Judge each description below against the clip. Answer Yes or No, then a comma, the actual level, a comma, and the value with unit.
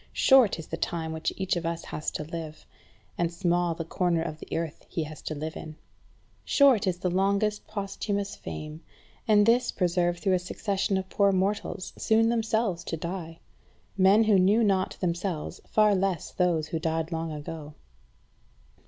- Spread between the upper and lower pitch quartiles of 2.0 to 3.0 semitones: No, average, 3.6 semitones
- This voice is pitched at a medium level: Yes, medium, 180 Hz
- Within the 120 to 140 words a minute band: No, average, 170 wpm